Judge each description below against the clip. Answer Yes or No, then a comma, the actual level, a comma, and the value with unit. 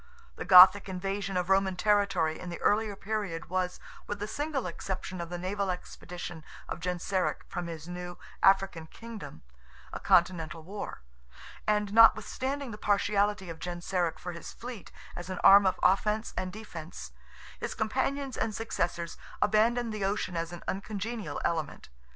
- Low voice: No, high, 190 Hz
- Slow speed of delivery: No, average, 150 wpm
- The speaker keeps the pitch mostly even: No, average, 3.1 semitones